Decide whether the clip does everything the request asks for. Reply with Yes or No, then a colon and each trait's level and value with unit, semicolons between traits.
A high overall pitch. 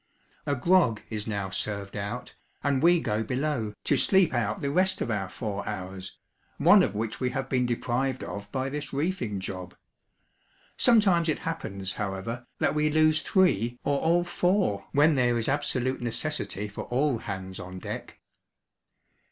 No: low, 125 Hz